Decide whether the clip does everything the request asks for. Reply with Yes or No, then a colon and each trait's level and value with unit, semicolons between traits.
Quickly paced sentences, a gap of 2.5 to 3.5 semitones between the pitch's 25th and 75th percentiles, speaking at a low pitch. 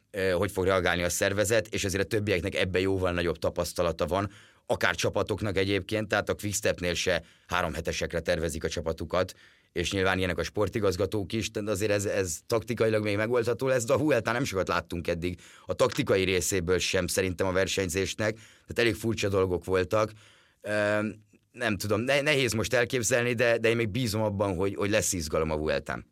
Yes: fast, 180 wpm; average, 3.0 semitones; low, 100 Hz